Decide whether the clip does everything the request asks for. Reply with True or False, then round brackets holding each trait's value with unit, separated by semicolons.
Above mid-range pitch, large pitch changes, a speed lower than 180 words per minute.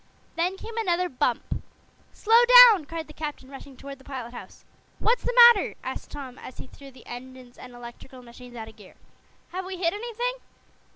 False (280 Hz; 7.2 semitones; 185 wpm)